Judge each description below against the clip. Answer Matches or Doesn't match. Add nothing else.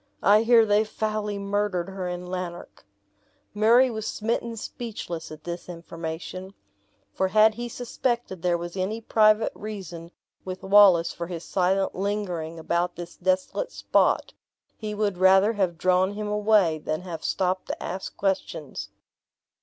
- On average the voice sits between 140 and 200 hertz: Matches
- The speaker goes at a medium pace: Matches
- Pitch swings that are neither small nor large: Matches